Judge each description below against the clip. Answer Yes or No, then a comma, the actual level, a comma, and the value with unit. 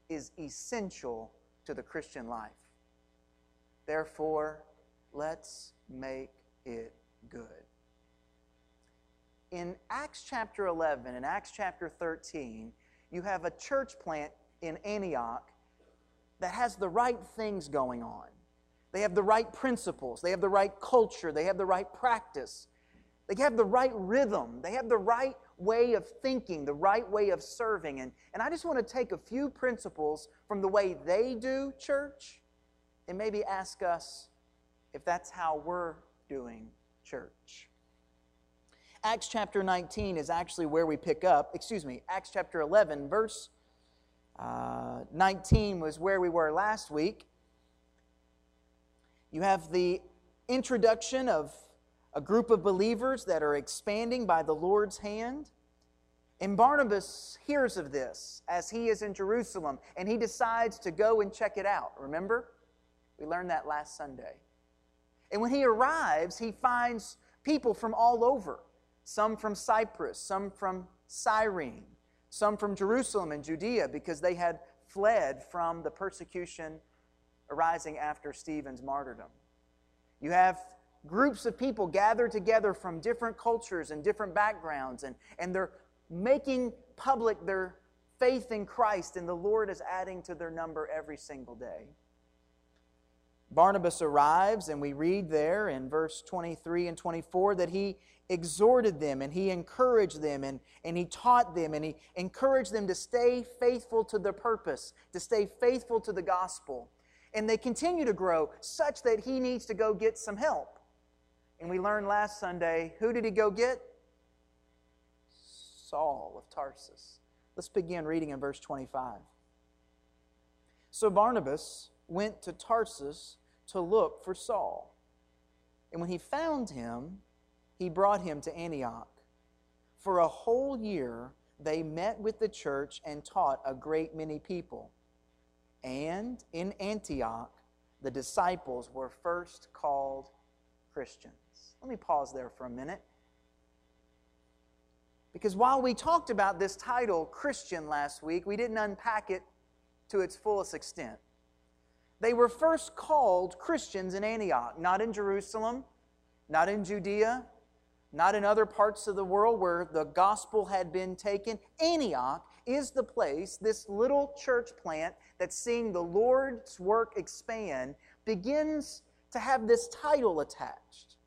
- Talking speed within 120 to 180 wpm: Yes, average, 140 wpm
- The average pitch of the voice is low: No, medium, 175 Hz